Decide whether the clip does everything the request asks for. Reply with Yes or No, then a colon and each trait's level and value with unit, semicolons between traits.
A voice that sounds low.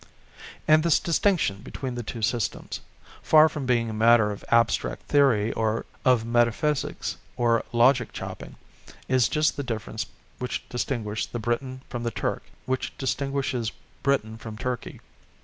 Yes: low, 120 Hz